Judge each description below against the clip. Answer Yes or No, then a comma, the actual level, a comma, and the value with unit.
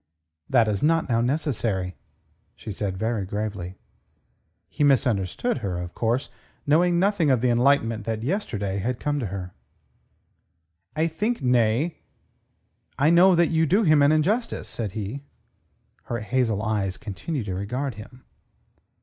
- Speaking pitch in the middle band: No, low, 120 Hz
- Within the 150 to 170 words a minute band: No, average, 140 wpm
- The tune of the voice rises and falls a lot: Yes, wide, 6.7 semitones